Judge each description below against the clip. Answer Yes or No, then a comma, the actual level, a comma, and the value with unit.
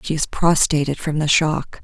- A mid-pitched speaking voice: Yes, medium, 155 Hz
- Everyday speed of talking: Yes, average, 195 wpm